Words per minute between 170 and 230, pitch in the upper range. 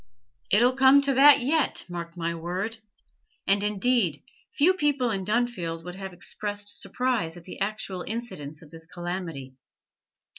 No: average, 150 wpm; high, 195 Hz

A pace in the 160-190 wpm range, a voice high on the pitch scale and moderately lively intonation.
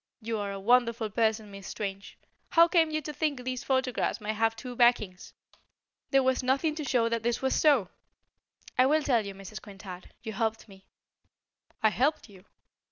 Yes: average, 180 wpm; high, 230 Hz; average, 4.0 semitones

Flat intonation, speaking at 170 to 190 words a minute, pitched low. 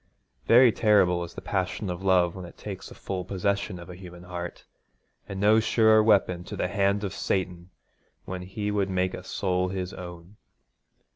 Yes: narrow, 2.2 semitones; average, 175 wpm; very low, 95 Hz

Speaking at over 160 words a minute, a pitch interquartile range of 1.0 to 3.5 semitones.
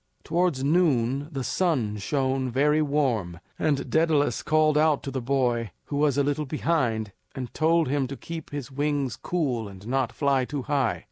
Yes: average, 175 wpm; average, 3.1 semitones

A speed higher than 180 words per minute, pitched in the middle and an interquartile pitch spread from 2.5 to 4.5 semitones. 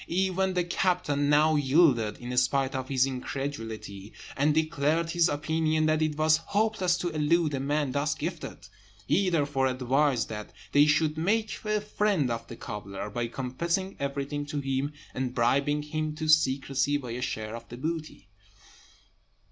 No: average, 160 wpm; medium, 145 Hz; average, 3.6 semitones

